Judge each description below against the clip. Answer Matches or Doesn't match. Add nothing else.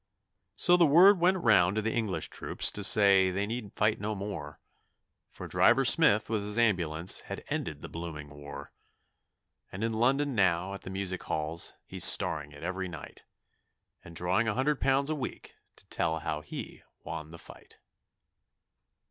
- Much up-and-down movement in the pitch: Matches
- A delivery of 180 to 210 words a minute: Doesn't match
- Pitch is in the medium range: Doesn't match